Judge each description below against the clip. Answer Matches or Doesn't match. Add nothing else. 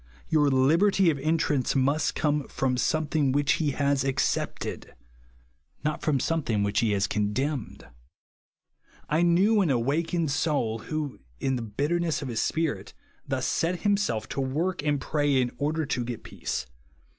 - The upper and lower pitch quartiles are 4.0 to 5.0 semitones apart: Doesn't match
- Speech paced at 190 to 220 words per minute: Doesn't match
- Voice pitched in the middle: Matches